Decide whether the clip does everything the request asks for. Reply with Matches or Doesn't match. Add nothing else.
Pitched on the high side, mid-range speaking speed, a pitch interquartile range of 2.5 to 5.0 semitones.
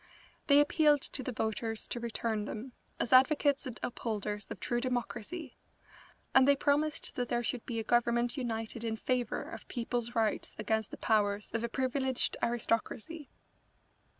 Matches